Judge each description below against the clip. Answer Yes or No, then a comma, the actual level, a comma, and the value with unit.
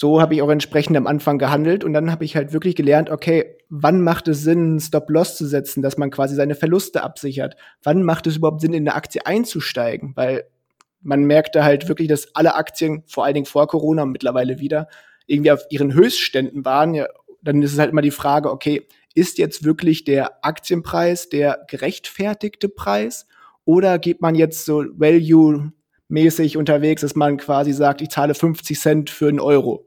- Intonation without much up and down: Yes, narrow, 2.0 semitones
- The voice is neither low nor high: Yes, medium, 155 Hz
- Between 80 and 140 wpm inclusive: No, fast, 190 wpm